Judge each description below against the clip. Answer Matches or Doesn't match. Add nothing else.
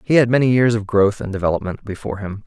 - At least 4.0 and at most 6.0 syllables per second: Doesn't match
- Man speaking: Matches